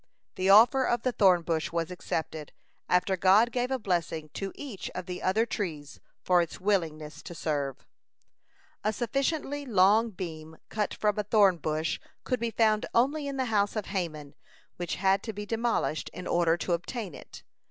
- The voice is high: Yes, high, 195 Hz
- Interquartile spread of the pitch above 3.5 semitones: Yes, average, 5.1 semitones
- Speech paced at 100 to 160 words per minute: No, average, 175 wpm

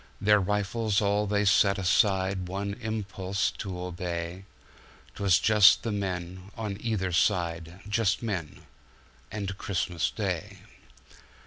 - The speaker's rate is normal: No, slow, 105 wpm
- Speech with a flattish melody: Yes, narrow, 2.1 semitones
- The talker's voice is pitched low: Yes, low, 100 Hz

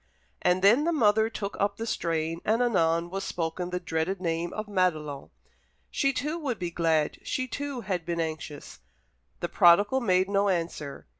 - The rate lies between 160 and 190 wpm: Yes, average, 170 wpm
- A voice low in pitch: No, medium, 185 Hz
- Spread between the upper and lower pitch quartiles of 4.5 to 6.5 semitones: Yes, average, 4.8 semitones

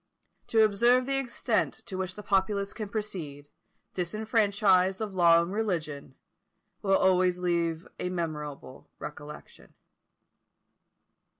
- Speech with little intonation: No, average, 4.0 semitones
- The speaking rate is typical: No, slow, 110 wpm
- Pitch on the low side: No, high, 190 Hz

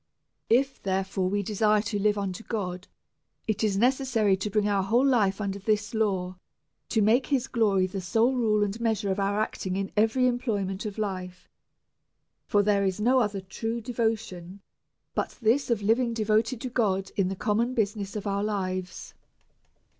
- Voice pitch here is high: Yes, high, 210 Hz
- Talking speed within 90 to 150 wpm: No, average, 175 wpm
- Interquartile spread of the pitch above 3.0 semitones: No, average, 2.7 semitones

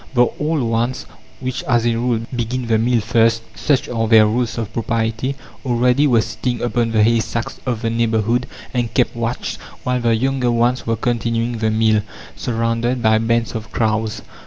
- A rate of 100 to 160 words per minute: No, average, 175 wpm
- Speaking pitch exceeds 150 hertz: No, low, 115 Hz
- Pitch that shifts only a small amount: Yes, narrow, 1.5 semitones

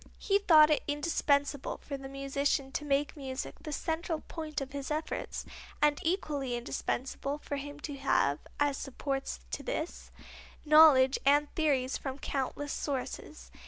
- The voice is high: Yes, very high, 285 Hz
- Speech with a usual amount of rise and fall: No, narrow, 1.9 semitones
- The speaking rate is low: No, average, 145 wpm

